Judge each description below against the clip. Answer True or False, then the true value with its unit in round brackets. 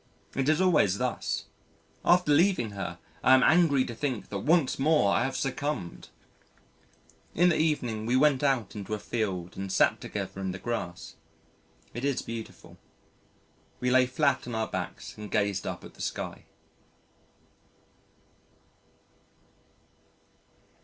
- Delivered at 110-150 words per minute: True (140 wpm)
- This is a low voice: True (125 Hz)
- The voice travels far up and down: True (6.3 semitones)